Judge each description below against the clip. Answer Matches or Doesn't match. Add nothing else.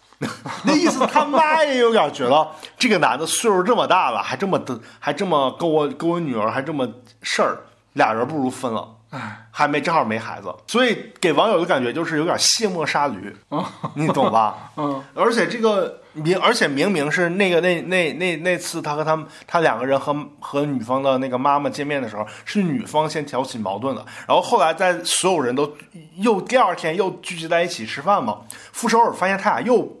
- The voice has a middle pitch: Matches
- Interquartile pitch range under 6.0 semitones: Matches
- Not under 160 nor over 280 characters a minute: Doesn't match